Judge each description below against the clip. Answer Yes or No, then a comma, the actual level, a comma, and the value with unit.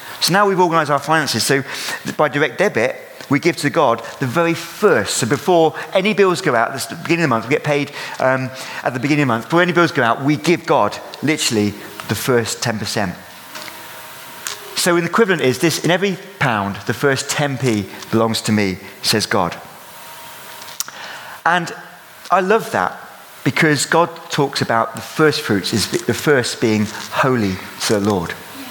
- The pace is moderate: Yes, average, 180 wpm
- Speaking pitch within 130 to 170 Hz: Yes, medium, 140 Hz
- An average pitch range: No, wide, 6.3 semitones